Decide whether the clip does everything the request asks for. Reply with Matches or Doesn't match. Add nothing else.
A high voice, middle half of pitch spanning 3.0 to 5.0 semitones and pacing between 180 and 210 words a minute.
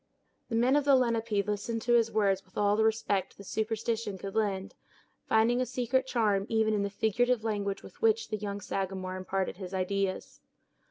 Doesn't match